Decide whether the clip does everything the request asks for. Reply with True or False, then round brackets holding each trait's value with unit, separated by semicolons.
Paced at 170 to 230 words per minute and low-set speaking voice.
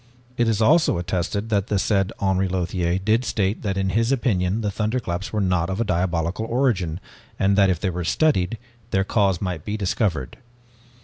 True (180 wpm; 95 Hz)